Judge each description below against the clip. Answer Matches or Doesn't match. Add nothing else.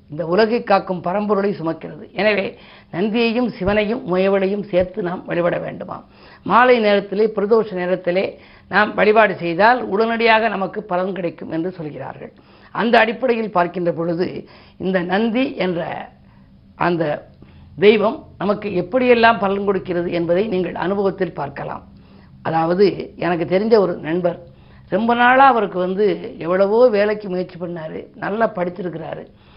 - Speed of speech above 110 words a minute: Matches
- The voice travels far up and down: Doesn't match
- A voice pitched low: Doesn't match